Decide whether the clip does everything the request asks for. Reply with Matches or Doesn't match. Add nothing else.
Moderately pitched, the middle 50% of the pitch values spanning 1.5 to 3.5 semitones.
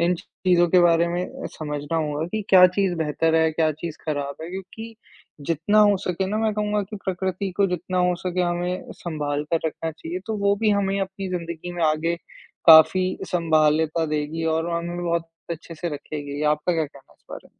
Matches